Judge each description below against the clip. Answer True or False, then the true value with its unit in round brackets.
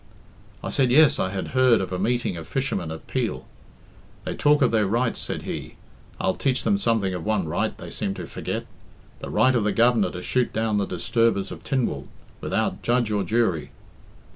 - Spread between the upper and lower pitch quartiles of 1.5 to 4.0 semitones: False (4.8 semitones)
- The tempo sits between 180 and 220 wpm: True (195 wpm)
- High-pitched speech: False (110 Hz)